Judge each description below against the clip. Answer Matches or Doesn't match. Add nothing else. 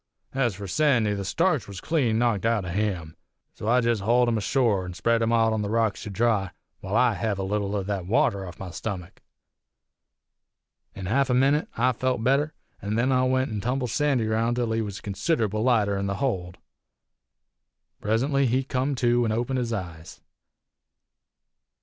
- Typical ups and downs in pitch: Matches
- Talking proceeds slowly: Doesn't match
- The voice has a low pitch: Matches